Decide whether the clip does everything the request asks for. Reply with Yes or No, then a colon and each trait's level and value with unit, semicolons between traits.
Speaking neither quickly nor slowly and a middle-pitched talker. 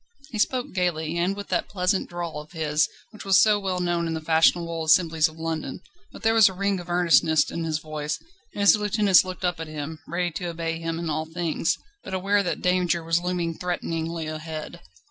No: fast, 210 wpm; medium, 170 Hz